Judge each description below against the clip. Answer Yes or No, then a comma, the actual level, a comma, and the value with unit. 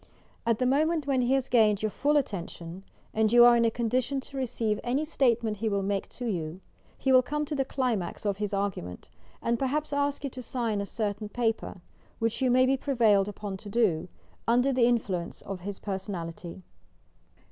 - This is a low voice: No, high, 230 Hz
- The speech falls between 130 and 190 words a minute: No, average, 200 wpm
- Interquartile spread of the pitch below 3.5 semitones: No, average, 4.3 semitones